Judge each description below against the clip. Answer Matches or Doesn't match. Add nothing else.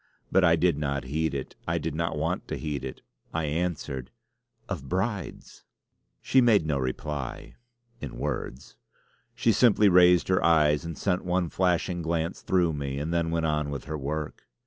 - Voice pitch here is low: Matches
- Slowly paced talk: Doesn't match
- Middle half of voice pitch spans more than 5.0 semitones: Doesn't match